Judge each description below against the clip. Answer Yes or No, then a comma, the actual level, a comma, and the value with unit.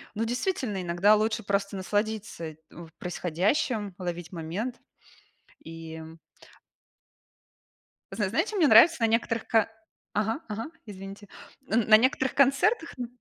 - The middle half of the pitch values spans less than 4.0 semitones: No, average, 4.6 semitones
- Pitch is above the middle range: Yes, high, 215 Hz